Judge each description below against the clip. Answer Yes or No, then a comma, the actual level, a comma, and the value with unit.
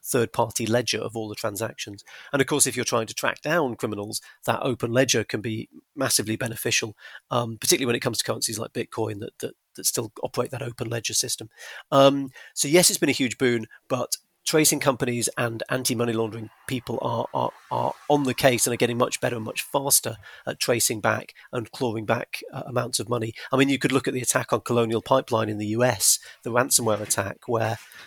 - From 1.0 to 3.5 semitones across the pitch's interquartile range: Yes, average, 2.7 semitones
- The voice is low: Yes, low, 120 Hz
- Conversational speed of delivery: No, fast, 220 wpm